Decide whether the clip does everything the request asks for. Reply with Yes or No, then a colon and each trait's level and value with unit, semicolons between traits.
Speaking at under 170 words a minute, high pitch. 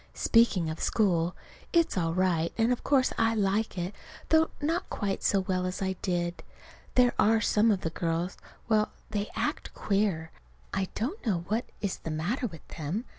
No: average, 175 wpm; high, 195 Hz